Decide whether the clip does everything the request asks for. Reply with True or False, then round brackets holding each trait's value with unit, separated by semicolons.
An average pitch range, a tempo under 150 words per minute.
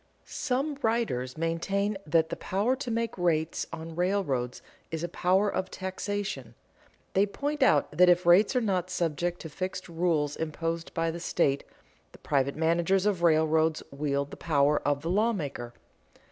False (4.1 semitones; 160 wpm)